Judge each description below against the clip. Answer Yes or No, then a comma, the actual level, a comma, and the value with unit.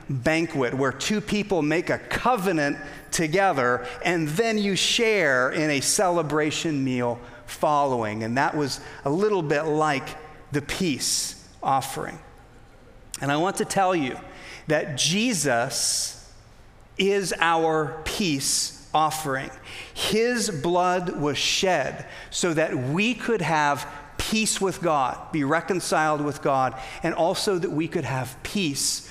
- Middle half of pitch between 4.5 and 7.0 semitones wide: Yes, average, 5.1 semitones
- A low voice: No, medium, 155 Hz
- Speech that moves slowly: Yes, slow, 130 wpm